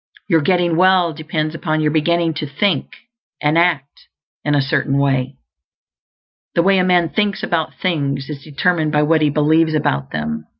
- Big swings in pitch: No, average, 3.1 semitones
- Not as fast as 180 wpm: Yes, average, 170 wpm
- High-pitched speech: No, medium, 155 Hz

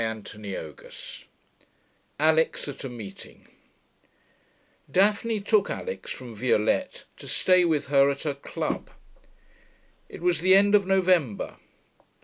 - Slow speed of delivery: Yes, slow, 125 wpm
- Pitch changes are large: Yes, wide, 7.7 semitones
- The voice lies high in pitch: No, medium, 155 Hz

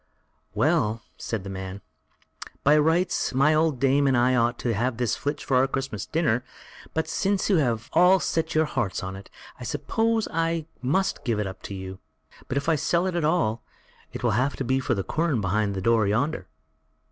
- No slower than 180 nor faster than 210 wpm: Yes, average, 195 wpm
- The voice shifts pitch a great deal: Yes, wide, 6.7 semitones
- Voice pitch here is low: Yes, low, 130 Hz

